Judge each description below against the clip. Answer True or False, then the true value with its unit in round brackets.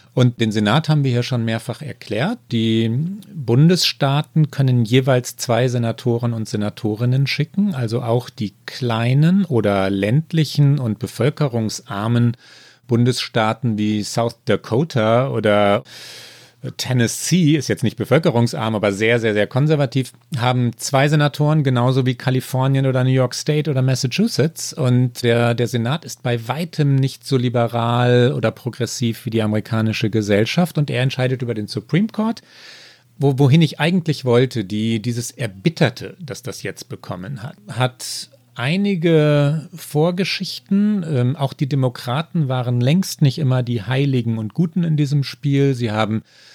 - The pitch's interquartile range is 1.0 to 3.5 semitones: False (4.2 semitones)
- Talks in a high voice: False (130 Hz)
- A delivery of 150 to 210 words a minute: False (140 wpm)